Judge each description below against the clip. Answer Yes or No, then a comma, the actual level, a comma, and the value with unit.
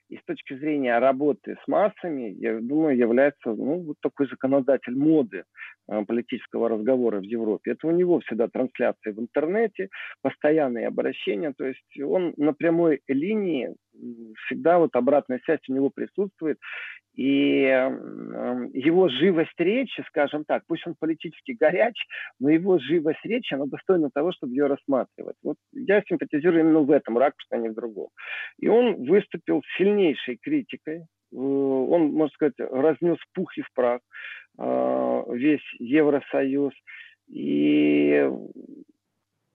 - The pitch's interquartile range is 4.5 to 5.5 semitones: Yes, average, 5.1 semitones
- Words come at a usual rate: Yes, average, 135 wpm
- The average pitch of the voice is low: No, medium, 145 Hz